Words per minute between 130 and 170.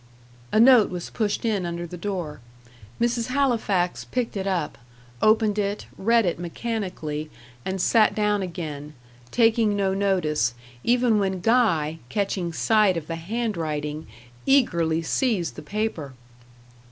Yes: slow, 135 wpm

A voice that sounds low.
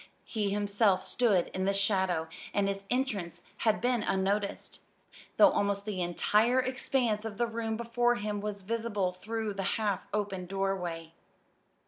No: high, 205 Hz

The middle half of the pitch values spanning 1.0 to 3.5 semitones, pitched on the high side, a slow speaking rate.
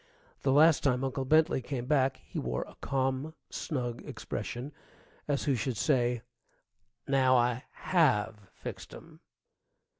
No: average, 2.7 semitones; low, 130 Hz; slow, 130 wpm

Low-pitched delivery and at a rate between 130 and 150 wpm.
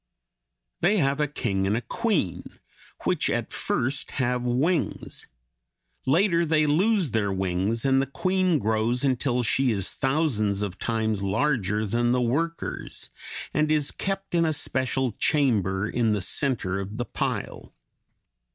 Yes: low, 125 Hz; average, 140 wpm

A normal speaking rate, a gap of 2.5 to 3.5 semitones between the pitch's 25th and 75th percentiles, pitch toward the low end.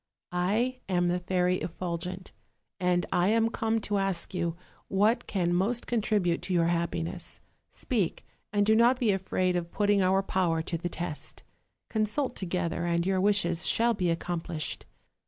No: average, 155 wpm; average, 3.1 semitones; medium, 185 Hz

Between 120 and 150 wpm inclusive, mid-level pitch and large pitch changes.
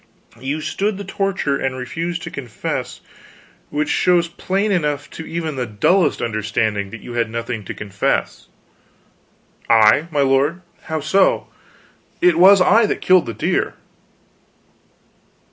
Yes: average, 140 wpm; medium, 150 Hz; wide, 7.2 semitones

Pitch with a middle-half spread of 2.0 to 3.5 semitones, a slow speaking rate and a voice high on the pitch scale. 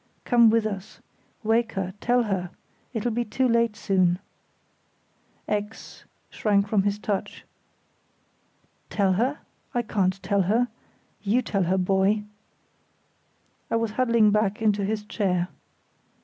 Yes: average, 2.8 semitones; slow, 125 wpm; high, 210 Hz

